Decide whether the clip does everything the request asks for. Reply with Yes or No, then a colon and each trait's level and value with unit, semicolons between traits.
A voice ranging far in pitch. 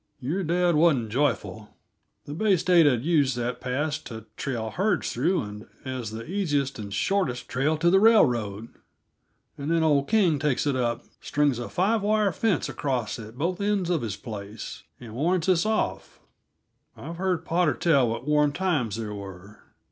Yes: wide, 6.9 semitones